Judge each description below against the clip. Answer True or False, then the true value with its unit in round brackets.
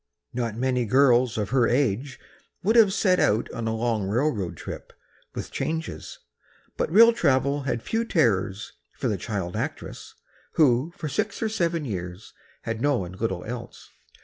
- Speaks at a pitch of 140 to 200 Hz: False (125 Hz)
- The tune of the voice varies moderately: False (6.1 semitones)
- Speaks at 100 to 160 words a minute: True (155 wpm)